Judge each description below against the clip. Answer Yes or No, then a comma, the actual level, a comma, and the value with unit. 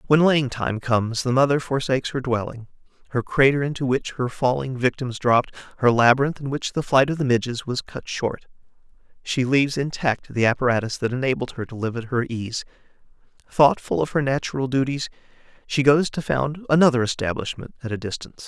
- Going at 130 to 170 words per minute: No, average, 180 wpm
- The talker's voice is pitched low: Yes, low, 130 Hz